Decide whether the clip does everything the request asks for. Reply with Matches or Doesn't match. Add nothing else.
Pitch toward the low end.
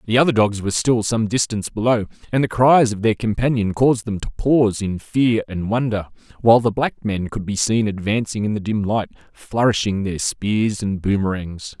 Matches